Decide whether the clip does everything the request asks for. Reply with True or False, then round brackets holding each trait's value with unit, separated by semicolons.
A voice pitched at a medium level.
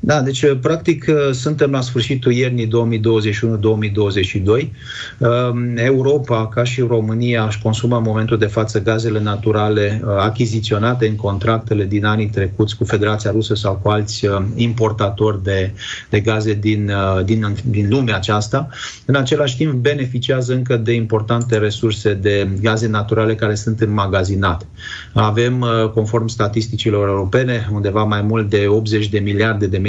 False (110 Hz)